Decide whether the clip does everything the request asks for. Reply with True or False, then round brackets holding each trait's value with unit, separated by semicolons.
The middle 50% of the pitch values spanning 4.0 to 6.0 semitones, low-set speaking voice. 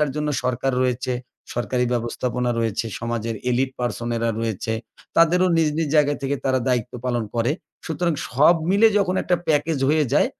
True (4.5 semitones; 130 Hz)